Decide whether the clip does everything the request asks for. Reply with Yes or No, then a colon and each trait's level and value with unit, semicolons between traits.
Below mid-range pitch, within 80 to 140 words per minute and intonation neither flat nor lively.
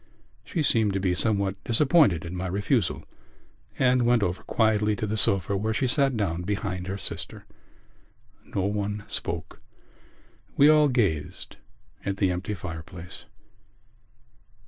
Yes: low, 100 Hz; slow, 135 wpm; average, 3.8 semitones